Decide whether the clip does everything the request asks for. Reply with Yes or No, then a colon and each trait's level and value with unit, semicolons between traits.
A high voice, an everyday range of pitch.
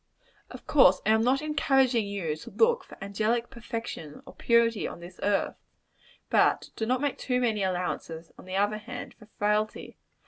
Yes: high, 220 Hz; average, 4.1 semitones